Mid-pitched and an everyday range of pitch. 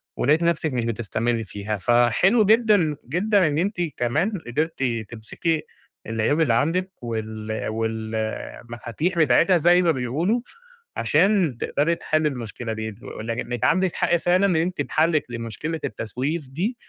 No: medium, 145 Hz; wide, 7.1 semitones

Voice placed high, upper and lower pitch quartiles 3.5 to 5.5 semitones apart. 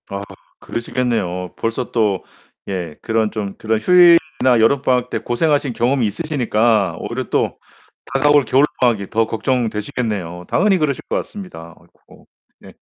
No: low, 115 Hz; average, 4.6 semitones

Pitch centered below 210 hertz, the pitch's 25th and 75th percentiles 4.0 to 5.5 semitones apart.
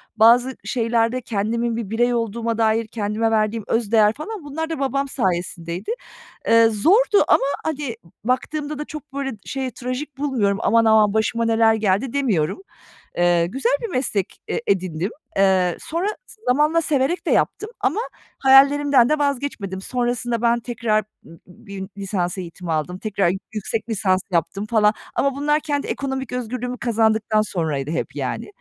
No: high, 230 Hz; average, 5.0 semitones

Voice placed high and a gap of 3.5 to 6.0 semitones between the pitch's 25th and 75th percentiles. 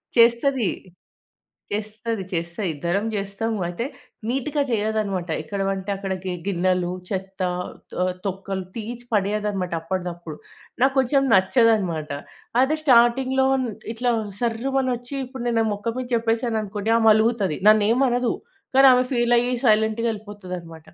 Yes: high, 215 Hz; average, 3.9 semitones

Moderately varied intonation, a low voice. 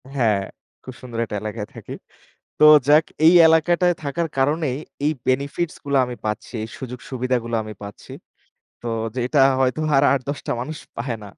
Yes: average, 4.3 semitones; low, 130 Hz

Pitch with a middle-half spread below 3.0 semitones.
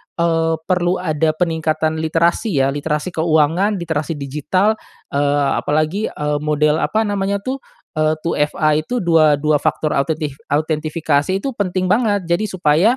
No: average, 3.4 semitones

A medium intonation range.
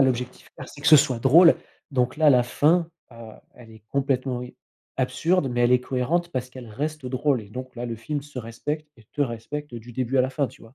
Yes: average, 3.3 semitones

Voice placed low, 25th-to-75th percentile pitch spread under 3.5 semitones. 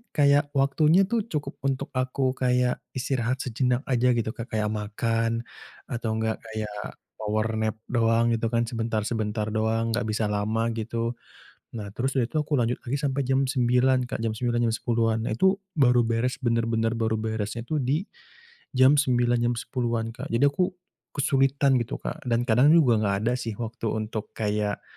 Yes: low, 120 Hz; narrow, 2.6 semitones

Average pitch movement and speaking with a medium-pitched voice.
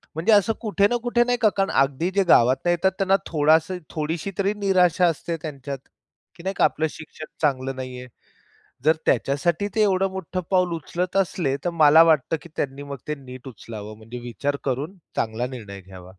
No: wide, 5.9 semitones; medium, 155 Hz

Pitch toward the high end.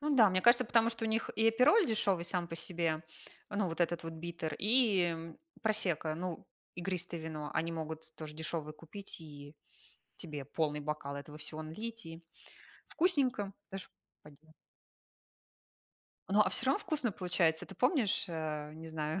No: medium, 170 Hz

